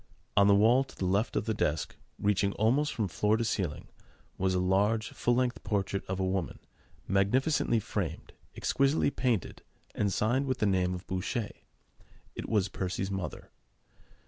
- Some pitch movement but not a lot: Yes, average, 3.6 semitones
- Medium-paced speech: Yes, average, 165 wpm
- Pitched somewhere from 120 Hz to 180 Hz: No, low, 100 Hz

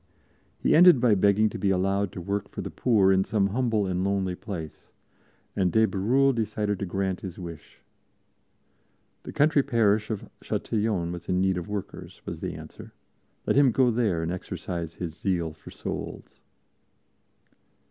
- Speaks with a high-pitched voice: No, low, 100 Hz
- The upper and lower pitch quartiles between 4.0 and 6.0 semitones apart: No, average, 3.4 semitones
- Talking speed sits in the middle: Yes, average, 165 wpm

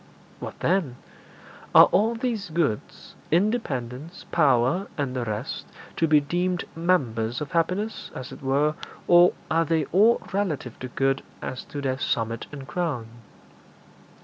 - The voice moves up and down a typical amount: No, wide, 5.7 semitones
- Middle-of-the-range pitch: Yes, medium, 150 Hz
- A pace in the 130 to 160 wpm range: Yes, average, 140 wpm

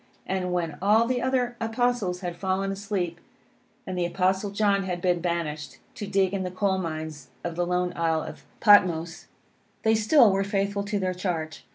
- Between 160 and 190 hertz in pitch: Yes, medium, 185 Hz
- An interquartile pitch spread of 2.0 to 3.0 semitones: Yes, average, 2.7 semitones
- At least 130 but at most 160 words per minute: No, average, 180 wpm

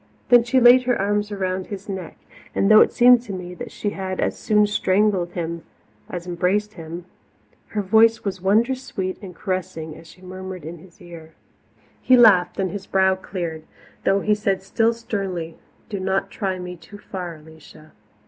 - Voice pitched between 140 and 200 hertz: Yes, high, 190 Hz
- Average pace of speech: Yes, average, 175 wpm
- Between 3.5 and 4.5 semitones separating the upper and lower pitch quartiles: No, average, 2.8 semitones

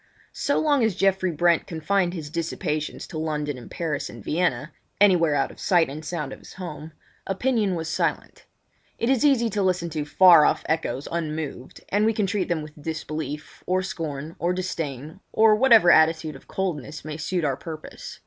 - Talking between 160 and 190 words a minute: Yes, average, 175 wpm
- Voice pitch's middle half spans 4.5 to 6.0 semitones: No, average, 3.7 semitones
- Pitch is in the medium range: Yes, medium, 165 Hz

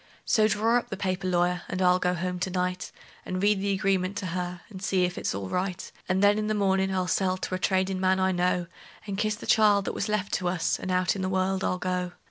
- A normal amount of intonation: No, narrow, 1.3 semitones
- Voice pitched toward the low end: No, medium, 185 Hz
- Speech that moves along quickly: Yes, fast, 260 wpm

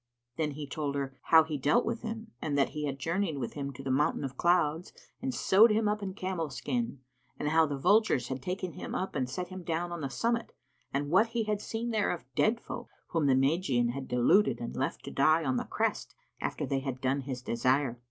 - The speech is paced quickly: Yes, fast, 235 wpm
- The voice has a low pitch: No, medium, 150 Hz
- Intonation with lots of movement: Yes, wide, 5.9 semitones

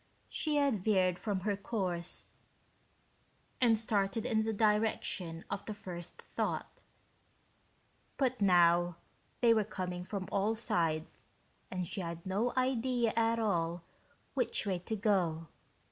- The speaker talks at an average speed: No, slow, 130 wpm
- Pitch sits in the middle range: No, high, 200 Hz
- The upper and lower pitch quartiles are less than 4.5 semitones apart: Yes, average, 4.1 semitones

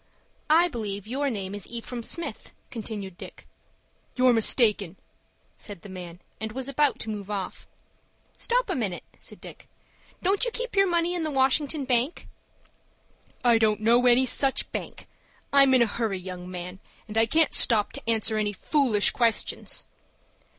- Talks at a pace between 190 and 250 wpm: No, average, 160 wpm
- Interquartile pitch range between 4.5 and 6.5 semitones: Yes, average, 5.1 semitones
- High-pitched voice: Yes, high, 230 Hz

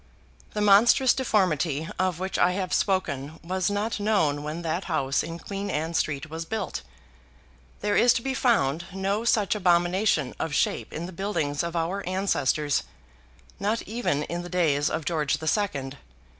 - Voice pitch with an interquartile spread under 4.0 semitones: No, average, 4.6 semitones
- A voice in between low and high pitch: Yes, medium, 175 Hz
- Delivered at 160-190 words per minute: Yes, average, 165 wpm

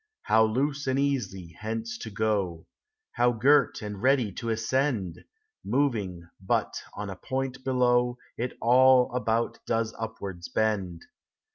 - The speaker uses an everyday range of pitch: Yes, average, 4.1 semitones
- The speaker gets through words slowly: Yes, slow, 130 wpm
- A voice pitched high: No, low, 115 Hz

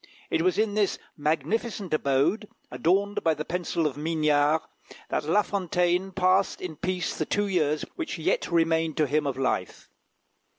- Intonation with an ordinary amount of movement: Yes, average, 4.1 semitones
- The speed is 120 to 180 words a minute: Yes, average, 160 wpm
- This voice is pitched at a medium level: Yes, medium, 165 Hz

